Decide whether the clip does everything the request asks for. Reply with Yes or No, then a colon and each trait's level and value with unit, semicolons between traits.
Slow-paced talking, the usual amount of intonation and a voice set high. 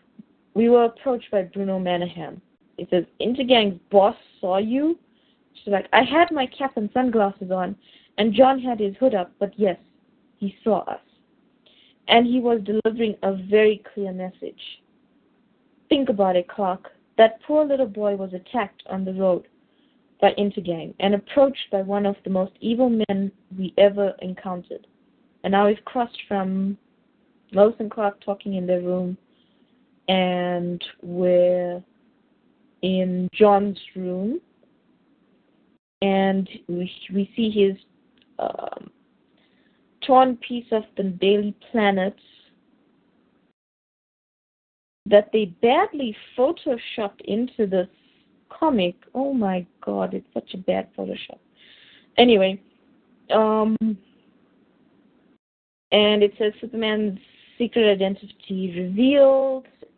Yes: slow, 120 wpm; average, 4.6 semitones; high, 215 Hz